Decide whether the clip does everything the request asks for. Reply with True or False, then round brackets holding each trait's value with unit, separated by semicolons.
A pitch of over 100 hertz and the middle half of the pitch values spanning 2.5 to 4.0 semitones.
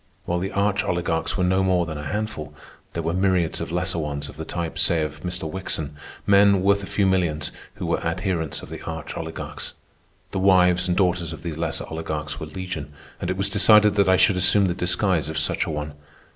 False (90 Hz; 3.0 semitones)